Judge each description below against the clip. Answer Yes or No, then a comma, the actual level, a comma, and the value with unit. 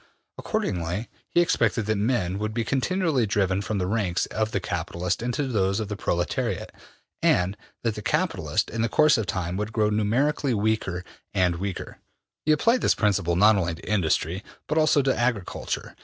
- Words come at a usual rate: Yes, average, 175 wpm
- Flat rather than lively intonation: No, average, 4.3 semitones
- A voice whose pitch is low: Yes, low, 105 Hz